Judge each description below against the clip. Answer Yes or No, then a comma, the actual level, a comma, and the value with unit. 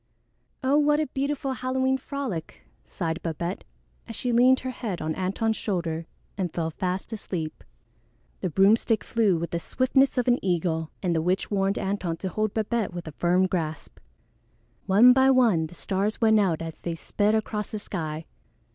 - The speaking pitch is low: No, high, 195 Hz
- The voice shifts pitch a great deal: Yes, wide, 6.0 semitones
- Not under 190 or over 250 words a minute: No, average, 175 wpm